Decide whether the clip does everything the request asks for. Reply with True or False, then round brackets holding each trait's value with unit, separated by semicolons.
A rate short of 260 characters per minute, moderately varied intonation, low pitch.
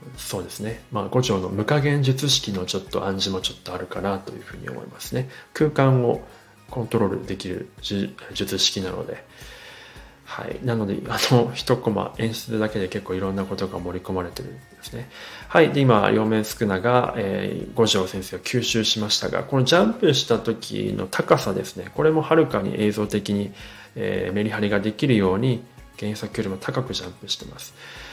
False (365 characters per minute; 3.9 semitones; 110 Hz)